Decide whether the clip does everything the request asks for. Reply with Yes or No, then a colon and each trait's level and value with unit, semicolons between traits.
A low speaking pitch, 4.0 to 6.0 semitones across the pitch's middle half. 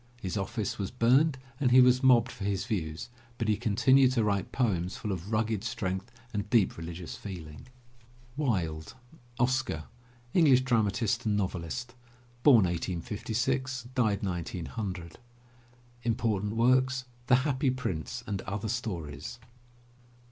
Yes: low, 110 Hz; average, 5.1 semitones